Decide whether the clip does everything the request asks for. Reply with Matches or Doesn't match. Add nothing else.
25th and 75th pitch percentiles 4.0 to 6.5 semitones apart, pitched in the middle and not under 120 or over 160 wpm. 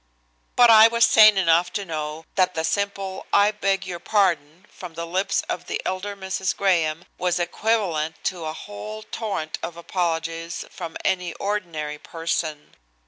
Doesn't match